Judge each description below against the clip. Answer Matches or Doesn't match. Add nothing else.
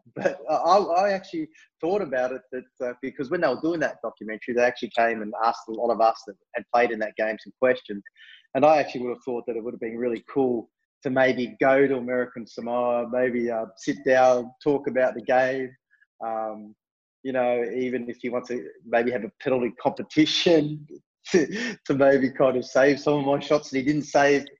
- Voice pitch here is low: Matches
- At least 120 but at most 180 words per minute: Doesn't match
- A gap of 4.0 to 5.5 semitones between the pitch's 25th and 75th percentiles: Doesn't match